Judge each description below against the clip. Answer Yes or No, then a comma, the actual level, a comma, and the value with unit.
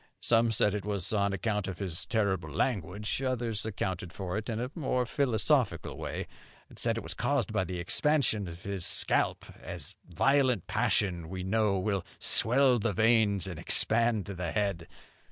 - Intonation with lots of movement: No, average, 3.8 semitones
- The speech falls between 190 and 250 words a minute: No, average, 170 wpm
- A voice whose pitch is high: No, low, 105 Hz